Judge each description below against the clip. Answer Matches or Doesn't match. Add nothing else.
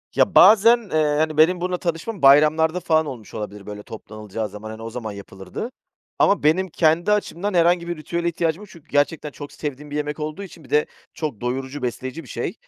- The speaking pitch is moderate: Matches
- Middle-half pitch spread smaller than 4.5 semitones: Doesn't match